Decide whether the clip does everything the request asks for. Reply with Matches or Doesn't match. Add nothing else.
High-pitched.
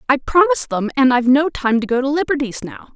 Matches